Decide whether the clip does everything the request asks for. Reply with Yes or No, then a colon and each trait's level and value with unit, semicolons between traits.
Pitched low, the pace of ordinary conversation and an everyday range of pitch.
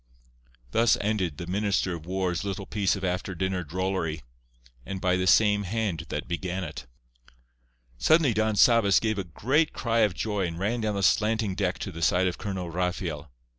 Yes: very low, 95 Hz; average, 180 wpm; average, 3.1 semitones